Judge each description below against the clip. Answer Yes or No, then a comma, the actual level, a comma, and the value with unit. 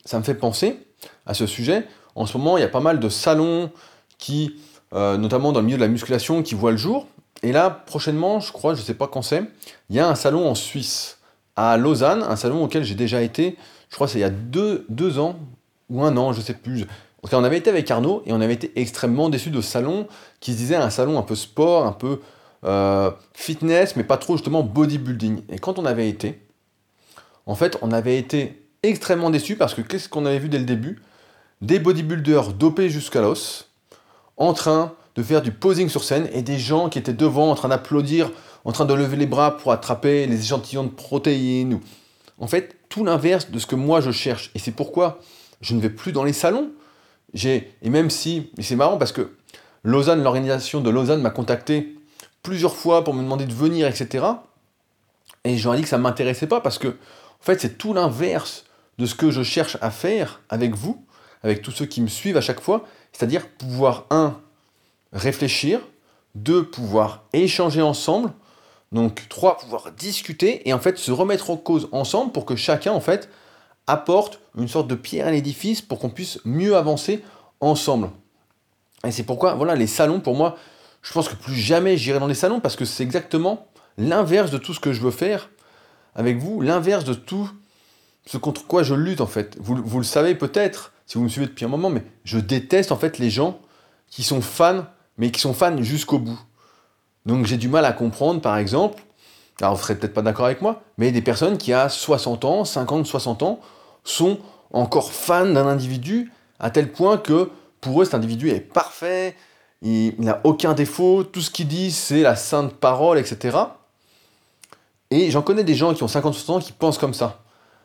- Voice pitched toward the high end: No, medium, 140 Hz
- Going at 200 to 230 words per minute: Yes, average, 210 wpm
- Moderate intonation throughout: No, wide, 5.7 semitones